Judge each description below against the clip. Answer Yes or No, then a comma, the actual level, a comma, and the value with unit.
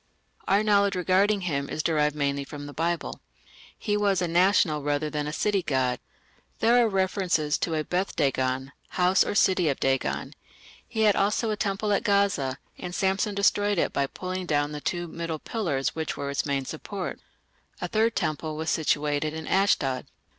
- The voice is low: No, medium, 170 Hz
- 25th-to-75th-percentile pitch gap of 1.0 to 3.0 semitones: No, average, 5.2 semitones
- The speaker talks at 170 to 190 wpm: Yes, average, 180 wpm